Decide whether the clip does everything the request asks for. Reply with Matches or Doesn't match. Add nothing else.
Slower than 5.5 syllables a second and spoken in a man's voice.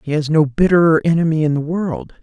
Doesn't match